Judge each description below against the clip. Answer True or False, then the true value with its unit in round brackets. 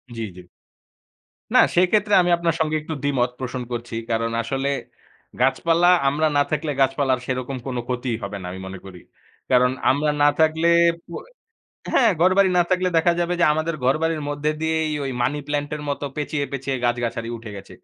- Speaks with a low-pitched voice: False (145 Hz)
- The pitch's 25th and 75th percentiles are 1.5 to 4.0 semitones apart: False (4.5 semitones)